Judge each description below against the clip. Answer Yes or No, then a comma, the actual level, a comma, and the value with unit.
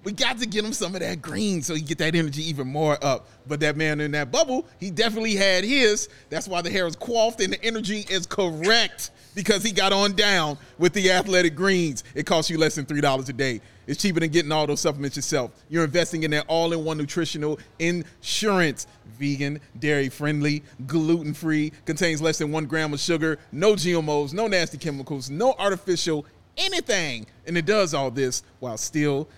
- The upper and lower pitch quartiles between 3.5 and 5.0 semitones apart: Yes, average, 4.4 semitones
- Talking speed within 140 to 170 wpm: No, average, 200 wpm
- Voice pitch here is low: No, medium, 160 Hz